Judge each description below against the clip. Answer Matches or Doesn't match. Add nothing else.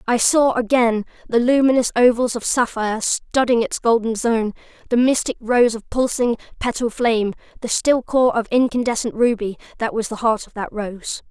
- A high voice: Matches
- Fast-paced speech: Doesn't match